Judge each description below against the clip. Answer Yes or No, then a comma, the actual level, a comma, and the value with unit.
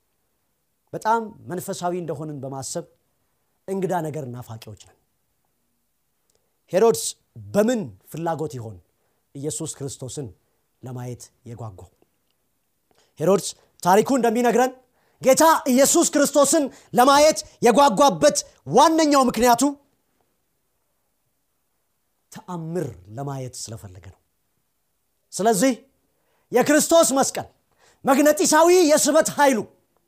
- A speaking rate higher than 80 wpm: No, slow, 70 wpm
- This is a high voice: Yes, high, 200 Hz